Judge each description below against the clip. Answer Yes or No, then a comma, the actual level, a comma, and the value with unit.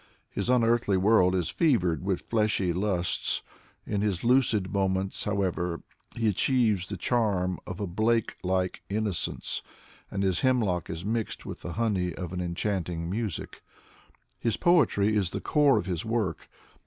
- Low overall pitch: Yes, low, 100 Hz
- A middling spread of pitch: Yes, average, 3.8 semitones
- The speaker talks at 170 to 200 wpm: No, average, 155 wpm